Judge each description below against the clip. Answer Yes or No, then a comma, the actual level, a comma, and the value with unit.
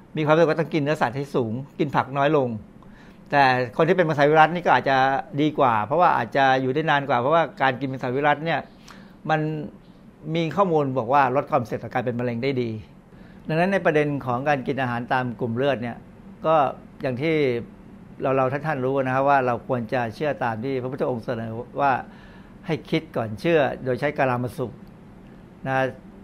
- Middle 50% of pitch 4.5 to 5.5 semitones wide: No, average, 3.6 semitones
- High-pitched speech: No, medium, 140 Hz